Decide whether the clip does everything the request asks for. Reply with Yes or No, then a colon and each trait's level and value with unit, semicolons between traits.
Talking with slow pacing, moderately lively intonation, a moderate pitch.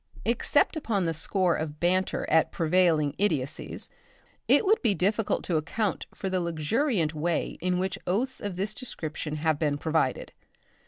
No: average, 155 wpm; average, 4.4 semitones; medium, 175 Hz